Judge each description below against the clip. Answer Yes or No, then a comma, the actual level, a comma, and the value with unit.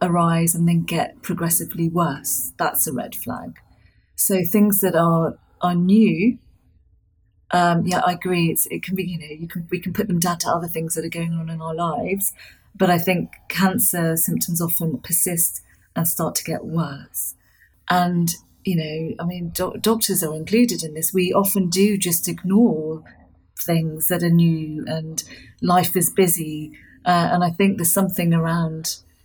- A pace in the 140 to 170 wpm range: No, average, 180 wpm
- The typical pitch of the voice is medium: Yes, medium, 170 Hz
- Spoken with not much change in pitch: Yes, narrow, 2.2 semitones